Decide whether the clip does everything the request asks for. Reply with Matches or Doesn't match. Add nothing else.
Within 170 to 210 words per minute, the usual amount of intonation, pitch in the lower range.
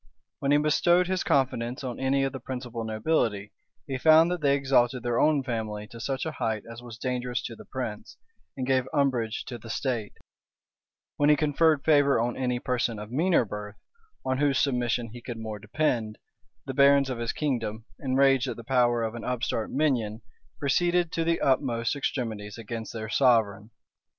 Matches